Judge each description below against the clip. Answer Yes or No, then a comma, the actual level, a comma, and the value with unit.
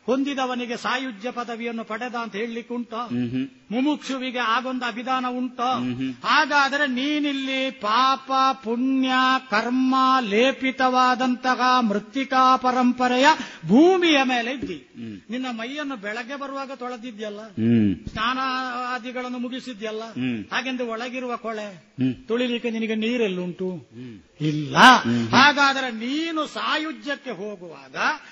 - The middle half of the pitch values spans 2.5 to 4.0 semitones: Yes, average, 2.9 semitones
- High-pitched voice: Yes, very high, 250 Hz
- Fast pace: No, average, 85 wpm